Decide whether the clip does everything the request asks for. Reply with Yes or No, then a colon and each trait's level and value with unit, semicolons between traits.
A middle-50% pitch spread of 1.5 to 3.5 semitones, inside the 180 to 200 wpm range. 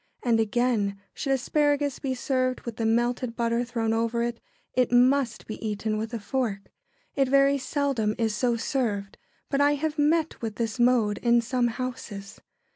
No: average, 2.9 semitones; average, 170 wpm